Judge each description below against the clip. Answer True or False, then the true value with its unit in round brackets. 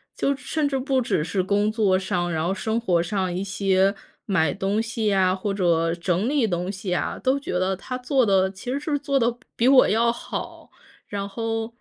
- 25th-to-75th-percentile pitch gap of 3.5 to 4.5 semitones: True (4.2 semitones)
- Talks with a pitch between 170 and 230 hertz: True (200 Hz)